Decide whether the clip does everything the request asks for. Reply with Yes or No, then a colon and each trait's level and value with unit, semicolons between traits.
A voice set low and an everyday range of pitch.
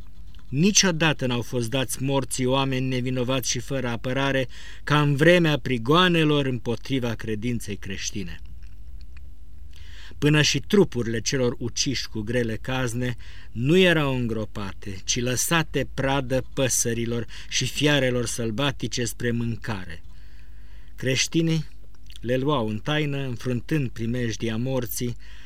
Yes: low, 120 Hz; average, 4.3 semitones